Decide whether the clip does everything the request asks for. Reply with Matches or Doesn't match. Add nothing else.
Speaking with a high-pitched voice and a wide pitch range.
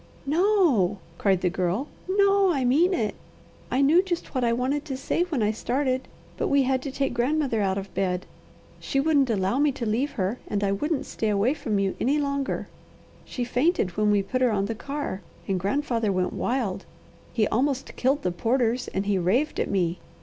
Matches